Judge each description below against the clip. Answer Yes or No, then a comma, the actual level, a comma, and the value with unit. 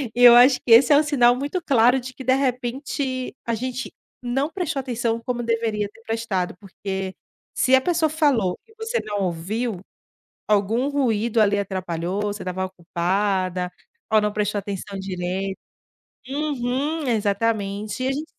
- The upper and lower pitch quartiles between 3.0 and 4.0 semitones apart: No, average, 4.7 semitones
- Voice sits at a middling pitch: No, high, 230 Hz